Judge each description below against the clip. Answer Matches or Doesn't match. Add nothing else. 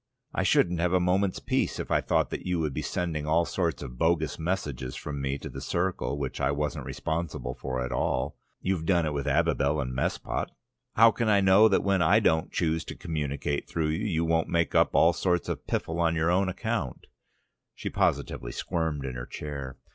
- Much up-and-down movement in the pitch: Doesn't match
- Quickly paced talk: Matches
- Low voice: Matches